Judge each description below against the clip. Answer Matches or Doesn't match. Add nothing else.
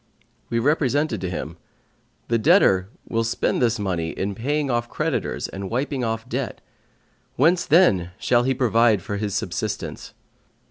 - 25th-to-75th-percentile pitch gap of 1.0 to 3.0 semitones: Doesn't match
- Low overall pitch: Matches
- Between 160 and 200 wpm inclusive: Doesn't match